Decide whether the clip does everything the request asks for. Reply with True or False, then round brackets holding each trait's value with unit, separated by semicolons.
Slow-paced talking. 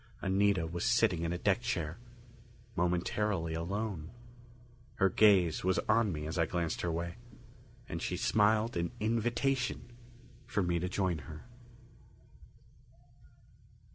True (125 wpm)